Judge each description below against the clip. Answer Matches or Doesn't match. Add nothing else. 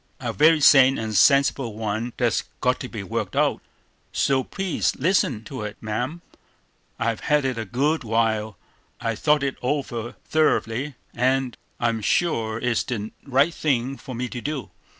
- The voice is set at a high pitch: Doesn't match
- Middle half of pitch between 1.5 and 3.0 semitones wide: Doesn't match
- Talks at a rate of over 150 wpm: Matches